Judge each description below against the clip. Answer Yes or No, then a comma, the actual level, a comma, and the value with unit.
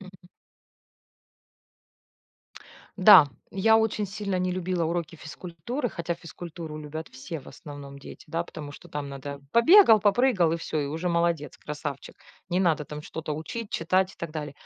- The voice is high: No, medium, 170 Hz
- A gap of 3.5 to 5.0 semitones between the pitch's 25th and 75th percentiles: Yes, average, 4.0 semitones